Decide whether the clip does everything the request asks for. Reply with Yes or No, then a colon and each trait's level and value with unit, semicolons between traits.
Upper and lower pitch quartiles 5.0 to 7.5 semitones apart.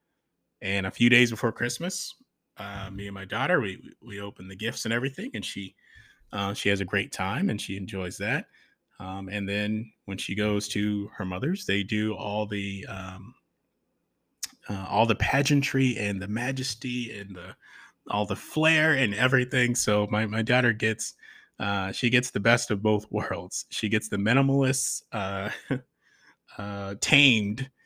No: average, 3.7 semitones